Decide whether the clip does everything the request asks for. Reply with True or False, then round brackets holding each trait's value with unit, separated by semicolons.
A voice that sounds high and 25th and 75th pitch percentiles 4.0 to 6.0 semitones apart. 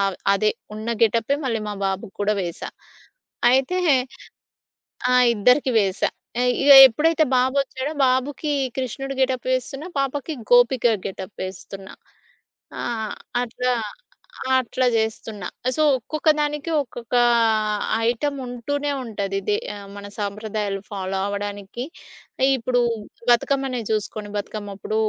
True (235 Hz; 4.5 semitones)